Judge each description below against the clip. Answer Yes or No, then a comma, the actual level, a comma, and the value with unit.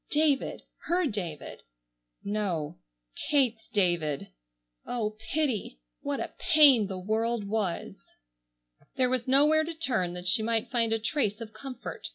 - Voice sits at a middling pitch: No, high, 220 Hz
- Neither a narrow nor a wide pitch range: No, wide, 6.1 semitones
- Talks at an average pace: No, slow, 130 wpm